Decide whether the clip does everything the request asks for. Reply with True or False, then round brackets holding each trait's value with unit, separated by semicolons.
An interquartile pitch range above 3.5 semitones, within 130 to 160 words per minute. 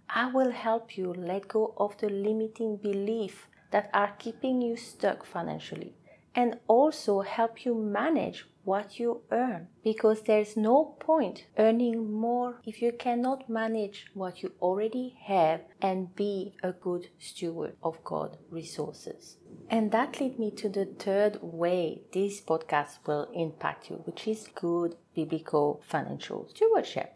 True (4.1 semitones; 145 wpm)